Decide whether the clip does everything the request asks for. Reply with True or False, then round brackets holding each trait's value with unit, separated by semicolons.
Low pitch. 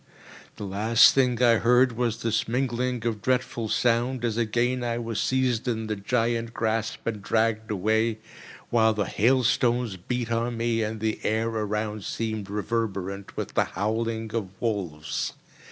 True (115 Hz)